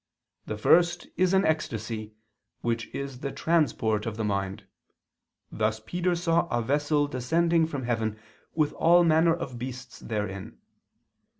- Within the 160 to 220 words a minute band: No, slow, 135 wpm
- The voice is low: Yes, low, 130 Hz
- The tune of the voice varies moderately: No, wide, 7.0 semitones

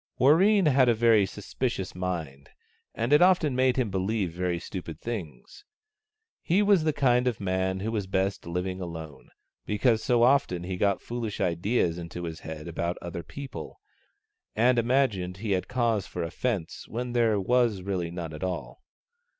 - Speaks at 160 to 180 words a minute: Yes, average, 165 wpm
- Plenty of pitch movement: Yes, wide, 5.7 semitones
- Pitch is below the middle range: Yes, low, 100 Hz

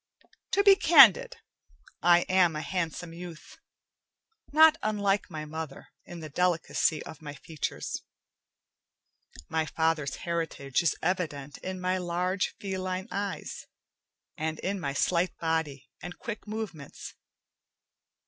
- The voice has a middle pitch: Yes, medium, 175 Hz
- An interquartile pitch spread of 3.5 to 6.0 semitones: No, average, 3.1 semitones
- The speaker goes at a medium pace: No, slow, 120 wpm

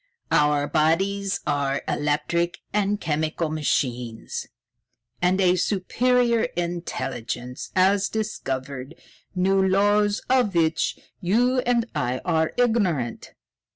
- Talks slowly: Yes, slow, 95 wpm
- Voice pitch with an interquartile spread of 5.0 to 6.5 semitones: Yes, wide, 5.6 semitones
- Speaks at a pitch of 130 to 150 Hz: No, medium, 175 Hz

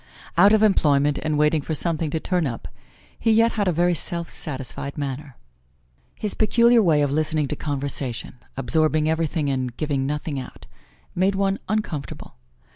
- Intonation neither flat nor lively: Yes, average, 4.1 semitones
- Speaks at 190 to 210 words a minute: No, average, 160 wpm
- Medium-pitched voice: Yes, medium, 155 Hz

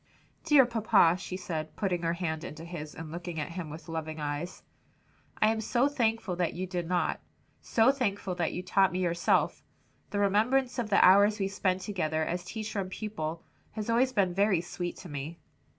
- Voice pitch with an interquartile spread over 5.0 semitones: No, average, 4.2 semitones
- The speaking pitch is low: No, medium, 185 Hz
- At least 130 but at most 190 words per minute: No, average, 200 wpm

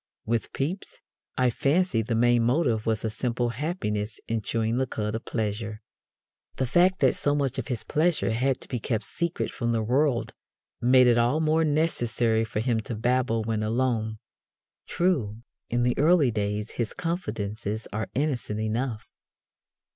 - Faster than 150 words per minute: Yes, average, 165 wpm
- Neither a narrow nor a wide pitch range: Yes, average, 3.7 semitones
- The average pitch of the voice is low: Yes, low, 120 Hz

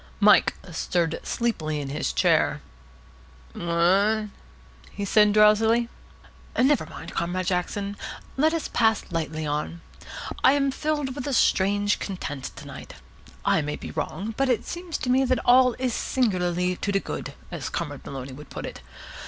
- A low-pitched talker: No, high, 205 Hz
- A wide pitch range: Yes, wide, 6.6 semitones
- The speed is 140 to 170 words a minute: Yes, average, 155 wpm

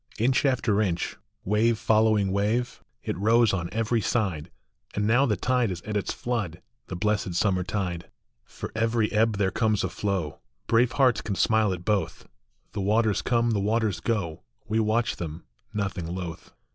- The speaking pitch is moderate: No, low, 105 Hz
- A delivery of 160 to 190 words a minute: Yes, average, 170 wpm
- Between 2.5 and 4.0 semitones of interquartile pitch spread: Yes, average, 3.2 semitones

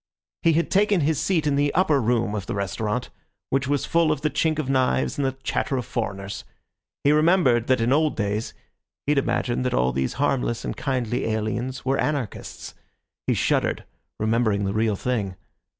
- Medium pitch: No, low, 130 Hz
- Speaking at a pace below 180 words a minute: No, average, 185 wpm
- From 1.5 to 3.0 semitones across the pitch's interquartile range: No, average, 5.1 semitones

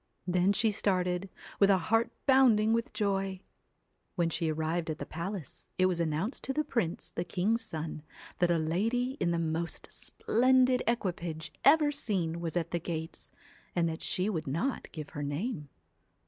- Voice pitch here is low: No, medium, 180 Hz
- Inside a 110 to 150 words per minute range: No, average, 170 wpm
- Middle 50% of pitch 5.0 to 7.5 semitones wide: Yes, wide, 5.4 semitones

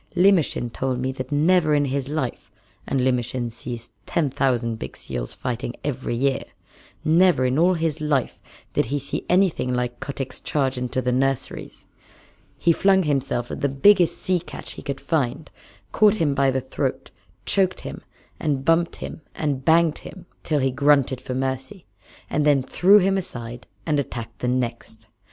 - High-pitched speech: No, low, 135 Hz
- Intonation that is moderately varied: Yes, average, 4.2 semitones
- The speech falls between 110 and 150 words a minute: No, average, 170 wpm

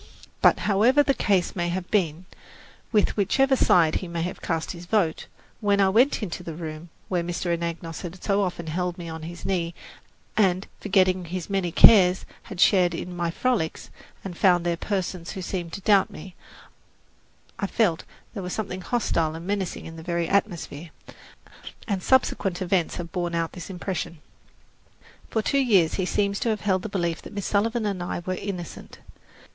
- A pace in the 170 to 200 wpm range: Yes, average, 185 wpm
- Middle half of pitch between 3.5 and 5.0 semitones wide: No, average, 2.8 semitones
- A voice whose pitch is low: No, medium, 180 Hz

